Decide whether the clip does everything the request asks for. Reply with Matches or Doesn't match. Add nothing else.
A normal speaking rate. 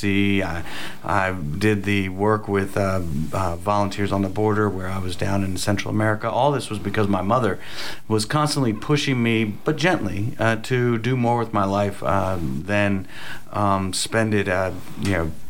Matches